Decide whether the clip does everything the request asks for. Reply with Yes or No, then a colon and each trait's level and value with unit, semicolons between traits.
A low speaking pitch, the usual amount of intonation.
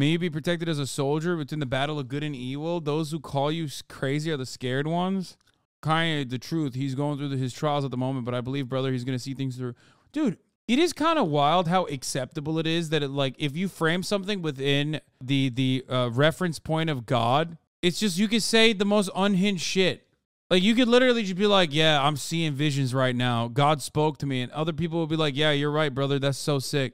No: medium, 150 Hz; average, 4.0 semitones